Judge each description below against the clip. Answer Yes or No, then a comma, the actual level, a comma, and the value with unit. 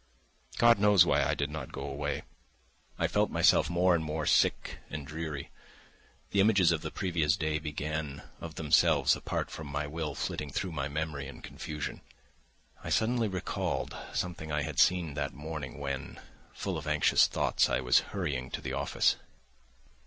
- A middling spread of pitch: Yes, average, 3.0 semitones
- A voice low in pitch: Yes, very low, 75 Hz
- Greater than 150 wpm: Yes, average, 165 wpm